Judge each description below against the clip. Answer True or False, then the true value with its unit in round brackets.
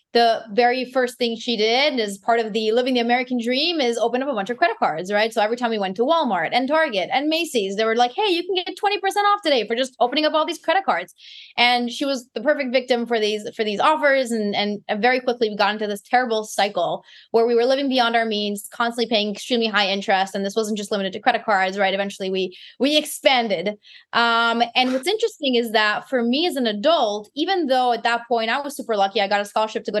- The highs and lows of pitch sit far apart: False (3.7 semitones)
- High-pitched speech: True (235 Hz)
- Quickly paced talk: True (250 wpm)